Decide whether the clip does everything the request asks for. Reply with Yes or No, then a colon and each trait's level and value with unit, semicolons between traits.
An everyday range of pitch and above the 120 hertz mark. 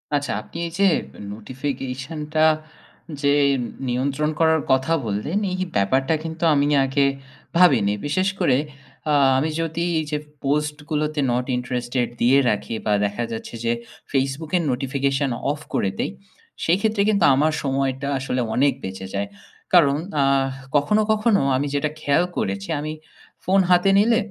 Yes: average, 3.7 semitones; medium, 140 Hz